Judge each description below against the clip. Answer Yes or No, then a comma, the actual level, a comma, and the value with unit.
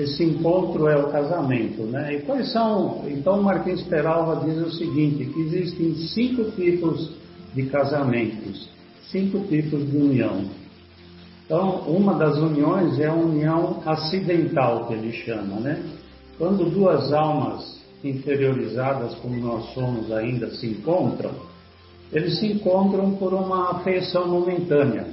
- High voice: No, medium, 155 Hz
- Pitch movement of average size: No, wide, 5.7 semitones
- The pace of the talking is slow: No, average, 130 wpm